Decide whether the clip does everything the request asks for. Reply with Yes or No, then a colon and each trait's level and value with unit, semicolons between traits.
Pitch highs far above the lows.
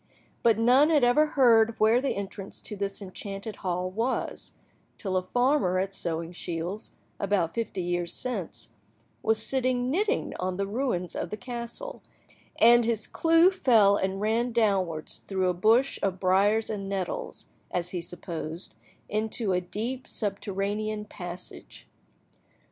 No: average, 4.3 semitones